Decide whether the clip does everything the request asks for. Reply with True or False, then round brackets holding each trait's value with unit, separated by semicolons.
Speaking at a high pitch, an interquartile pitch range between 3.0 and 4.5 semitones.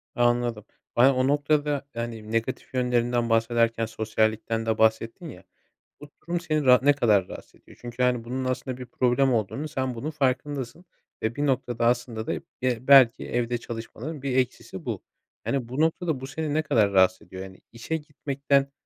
False (125 Hz; 3.3 semitones)